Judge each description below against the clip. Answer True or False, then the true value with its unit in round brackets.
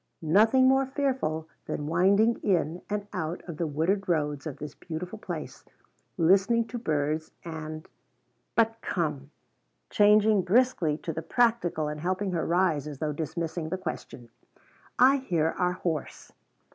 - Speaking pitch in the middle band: True (175 Hz)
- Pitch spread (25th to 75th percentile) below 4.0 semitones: False (5.0 semitones)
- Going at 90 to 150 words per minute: True (145 wpm)